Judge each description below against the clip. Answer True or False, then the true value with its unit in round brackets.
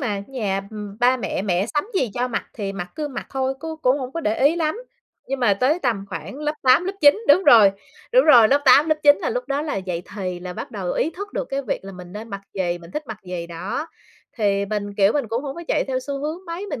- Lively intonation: True (6.8 semitones)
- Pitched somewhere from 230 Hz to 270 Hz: True (250 Hz)